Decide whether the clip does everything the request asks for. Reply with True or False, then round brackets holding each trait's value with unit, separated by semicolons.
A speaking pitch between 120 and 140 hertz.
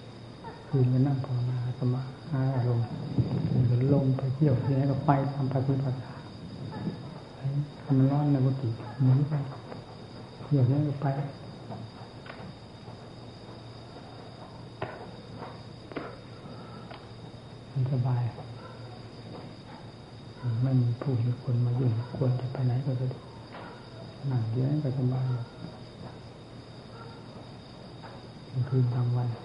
True (130 Hz)